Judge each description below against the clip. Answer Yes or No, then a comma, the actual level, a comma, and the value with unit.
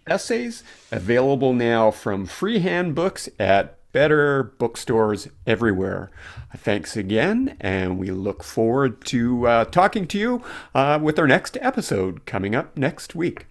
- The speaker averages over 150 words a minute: No, slow, 135 wpm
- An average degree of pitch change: No, wide, 8.1 semitones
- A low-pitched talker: Yes, low, 120 Hz